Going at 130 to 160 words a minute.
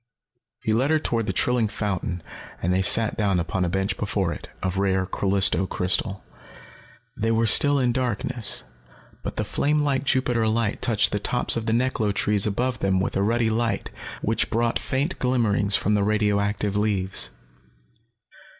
No: average, 170 wpm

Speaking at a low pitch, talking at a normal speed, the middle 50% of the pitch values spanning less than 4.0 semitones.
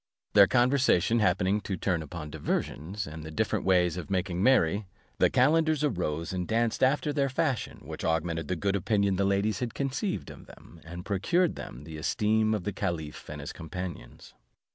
No: very low, 95 Hz; average, 180 wpm; wide, 5.6 semitones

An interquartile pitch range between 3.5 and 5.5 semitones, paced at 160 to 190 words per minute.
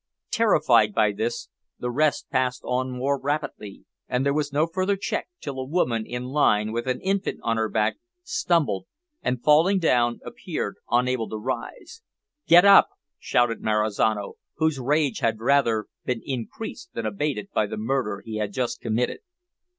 Yes: average, 5.1 semitones; average, 165 wpm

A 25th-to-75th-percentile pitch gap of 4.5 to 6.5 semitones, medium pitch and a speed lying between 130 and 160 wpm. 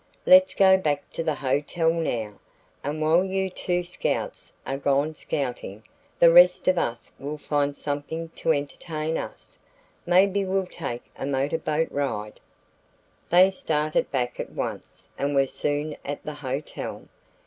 No: average, 3.7 semitones; medium, 150 Hz; average, 145 wpm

